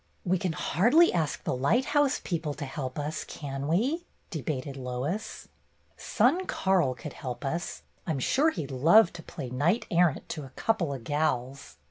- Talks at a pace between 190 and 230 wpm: No, average, 175 wpm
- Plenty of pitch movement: Yes, wide, 5.7 semitones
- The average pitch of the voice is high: No, medium, 155 Hz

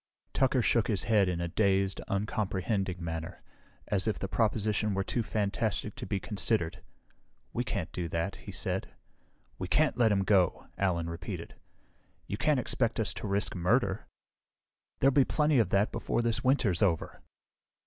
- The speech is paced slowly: No, average, 160 wpm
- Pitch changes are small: No, average, 3.5 semitones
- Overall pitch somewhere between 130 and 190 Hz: No, low, 100 Hz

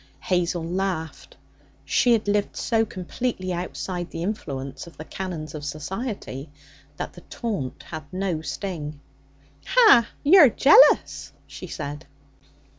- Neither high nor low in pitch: Yes, medium, 180 Hz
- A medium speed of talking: No, slow, 120 wpm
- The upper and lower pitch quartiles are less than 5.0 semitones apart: No, wide, 5.4 semitones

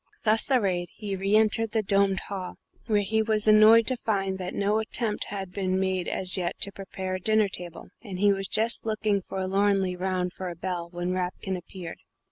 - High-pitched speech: Yes, high, 195 Hz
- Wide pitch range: No, narrow, 2.5 semitones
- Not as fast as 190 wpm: No, average, 195 wpm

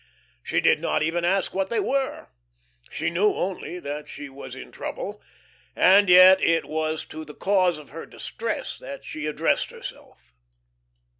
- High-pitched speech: No, medium, 175 Hz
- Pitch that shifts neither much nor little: Yes, average, 3.9 semitones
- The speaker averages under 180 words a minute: Yes, average, 160 wpm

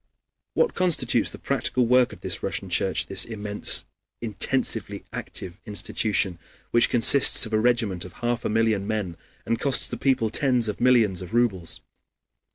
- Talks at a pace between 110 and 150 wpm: No, average, 160 wpm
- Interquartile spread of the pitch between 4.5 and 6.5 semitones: No, average, 3.0 semitones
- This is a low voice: Yes, low, 115 Hz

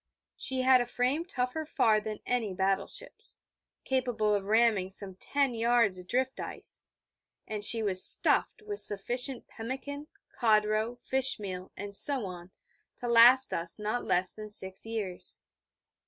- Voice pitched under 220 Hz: No, high, 225 Hz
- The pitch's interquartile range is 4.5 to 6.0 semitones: No, average, 4.1 semitones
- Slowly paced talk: No, average, 150 wpm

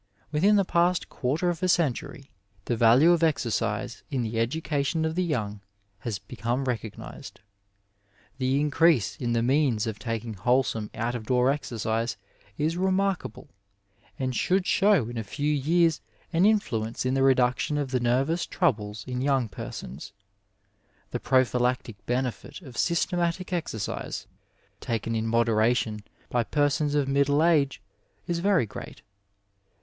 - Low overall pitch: Yes, low, 130 Hz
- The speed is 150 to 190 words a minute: No, average, 140 wpm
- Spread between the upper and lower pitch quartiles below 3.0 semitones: No, wide, 5.6 semitones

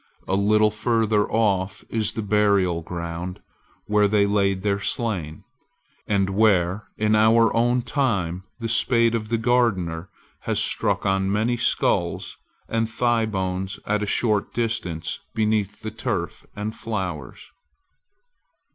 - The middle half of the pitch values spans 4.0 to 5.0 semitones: No, average, 2.9 semitones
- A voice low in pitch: Yes, low, 105 Hz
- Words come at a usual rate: No, slow, 130 wpm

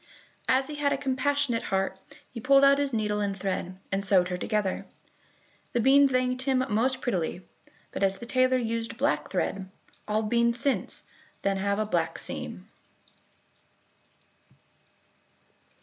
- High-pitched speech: Yes, high, 230 Hz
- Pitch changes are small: No, average, 4.8 semitones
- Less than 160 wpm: Yes, average, 145 wpm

